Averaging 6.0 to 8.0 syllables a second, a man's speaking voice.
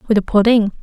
No: 6.9 syllables/s; female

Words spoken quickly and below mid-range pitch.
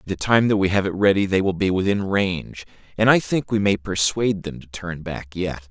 Yes: fast, 250 wpm; very low, 95 Hz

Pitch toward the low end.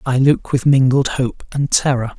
Yes: low, 130 Hz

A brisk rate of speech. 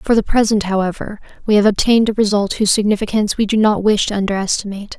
Yes: fast, 215 wpm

